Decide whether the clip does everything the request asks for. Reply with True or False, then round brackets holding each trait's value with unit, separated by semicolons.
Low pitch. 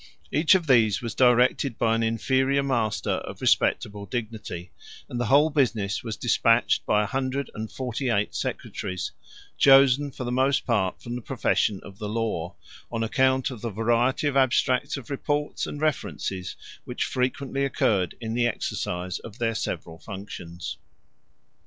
True (120 Hz)